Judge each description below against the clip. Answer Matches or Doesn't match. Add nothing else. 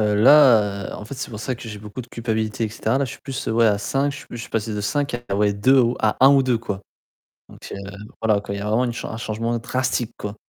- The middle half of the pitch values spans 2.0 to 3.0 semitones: Doesn't match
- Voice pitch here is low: Matches